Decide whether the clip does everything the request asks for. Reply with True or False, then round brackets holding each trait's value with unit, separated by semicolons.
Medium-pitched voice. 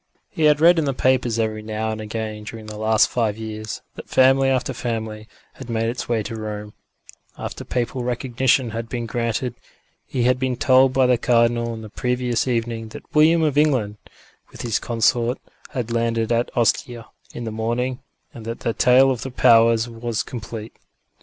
False (115 Hz)